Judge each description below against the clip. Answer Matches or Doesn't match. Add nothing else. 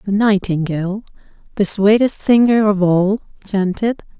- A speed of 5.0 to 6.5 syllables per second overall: Doesn't match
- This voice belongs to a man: Doesn't match